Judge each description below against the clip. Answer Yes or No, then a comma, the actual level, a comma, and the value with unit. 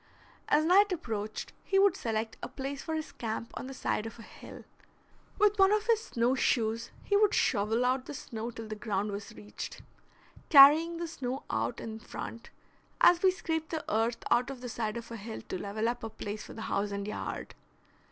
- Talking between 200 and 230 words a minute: Yes, fast, 205 wpm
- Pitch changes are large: Yes, wide, 6.5 semitones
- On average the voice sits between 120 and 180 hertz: No, high, 240 Hz